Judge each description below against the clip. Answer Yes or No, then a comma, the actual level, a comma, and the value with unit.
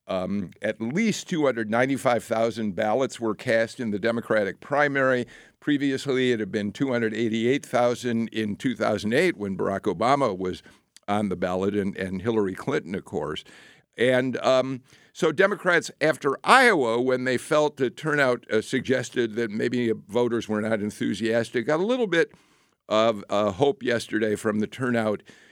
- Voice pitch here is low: Yes, low, 115 Hz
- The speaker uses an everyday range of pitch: Yes, average, 3.5 semitones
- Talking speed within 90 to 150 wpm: Yes, average, 145 wpm